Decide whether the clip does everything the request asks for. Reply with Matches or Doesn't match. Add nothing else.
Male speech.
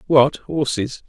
Matches